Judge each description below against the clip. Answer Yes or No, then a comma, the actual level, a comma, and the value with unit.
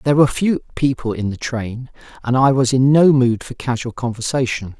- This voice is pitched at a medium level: No, low, 125 Hz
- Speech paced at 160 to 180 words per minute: No, average, 200 wpm